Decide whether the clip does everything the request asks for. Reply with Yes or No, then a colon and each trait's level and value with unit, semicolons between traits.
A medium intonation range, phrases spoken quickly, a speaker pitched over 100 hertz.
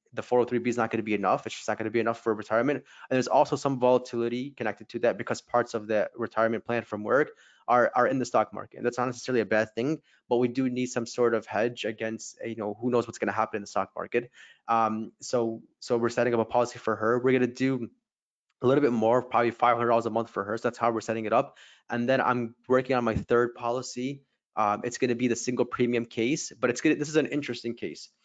No: narrow, 1.8 semitones; fast, 265 wpm; low, 120 Hz